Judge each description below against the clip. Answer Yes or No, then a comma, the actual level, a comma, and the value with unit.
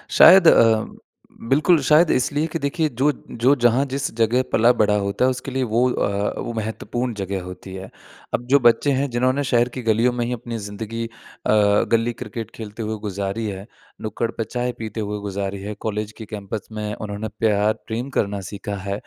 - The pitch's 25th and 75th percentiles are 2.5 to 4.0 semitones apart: Yes, average, 3.2 semitones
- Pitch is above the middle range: No, low, 115 Hz